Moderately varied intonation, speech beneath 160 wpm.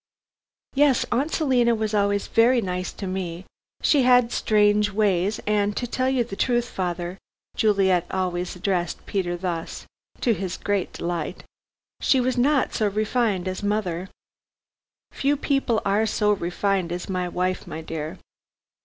Yes: average, 4.6 semitones; average, 150 wpm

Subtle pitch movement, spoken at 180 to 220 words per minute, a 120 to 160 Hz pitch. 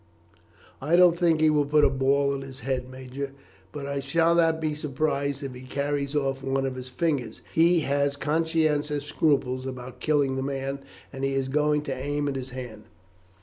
Yes: narrow, 2.1 semitones; average, 190 wpm; medium, 140 Hz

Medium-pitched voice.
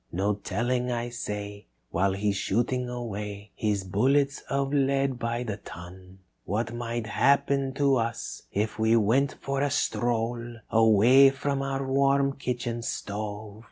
No: low, 120 Hz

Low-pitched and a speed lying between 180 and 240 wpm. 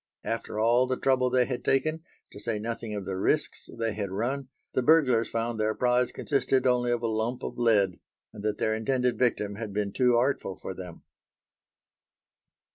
Yes: low, 115 Hz; average, 185 wpm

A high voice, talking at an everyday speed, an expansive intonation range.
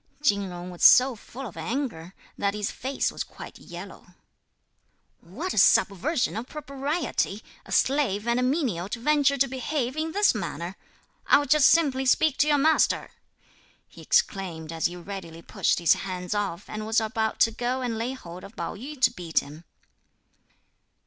Yes: high, 230 Hz; average, 170 wpm; wide, 6.5 semitones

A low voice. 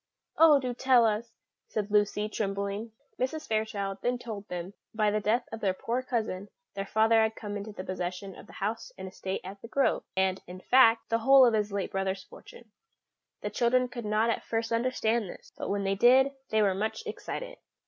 No: high, 215 Hz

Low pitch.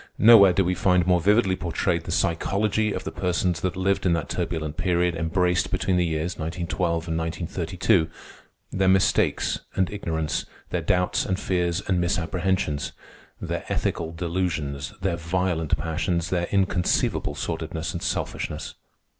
Yes: very low, 90 Hz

